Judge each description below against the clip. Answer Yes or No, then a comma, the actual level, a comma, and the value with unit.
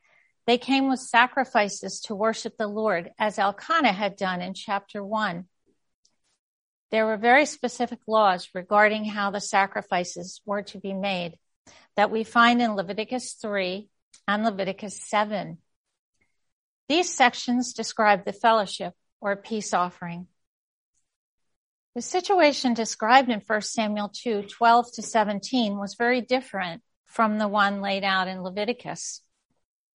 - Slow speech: Yes, slow, 130 wpm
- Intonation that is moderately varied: Yes, average, 3.2 semitones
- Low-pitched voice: No, high, 215 Hz